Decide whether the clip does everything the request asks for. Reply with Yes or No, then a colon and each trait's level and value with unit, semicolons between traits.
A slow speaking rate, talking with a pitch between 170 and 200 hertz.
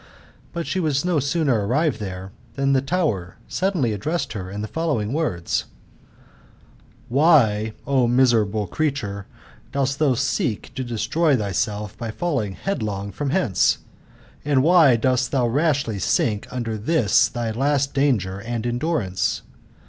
No: slow, 130 wpm; low, 125 Hz